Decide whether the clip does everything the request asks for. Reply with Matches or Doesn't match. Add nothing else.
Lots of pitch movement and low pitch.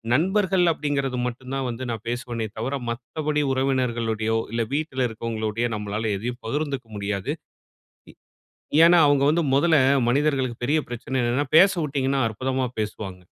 Doesn't match